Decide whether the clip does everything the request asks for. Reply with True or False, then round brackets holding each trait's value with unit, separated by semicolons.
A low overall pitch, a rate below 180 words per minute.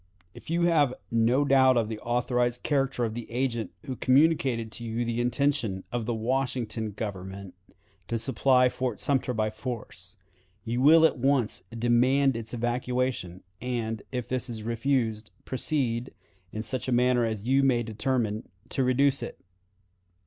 True (120 Hz; 155 wpm)